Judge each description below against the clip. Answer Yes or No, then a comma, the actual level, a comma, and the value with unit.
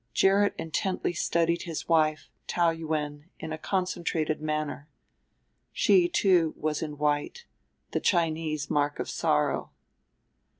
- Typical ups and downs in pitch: No, narrow, 2.3 semitones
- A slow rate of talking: Yes, slow, 120 wpm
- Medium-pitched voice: Yes, medium, 160 Hz